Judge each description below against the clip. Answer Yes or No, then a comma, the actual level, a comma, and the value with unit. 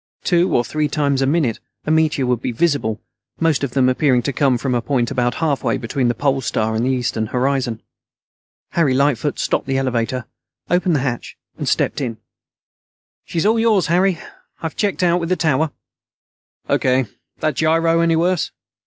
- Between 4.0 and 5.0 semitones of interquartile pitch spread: Yes, average, 4.6 semitones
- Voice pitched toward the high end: No, medium, 140 Hz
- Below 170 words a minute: No, average, 180 wpm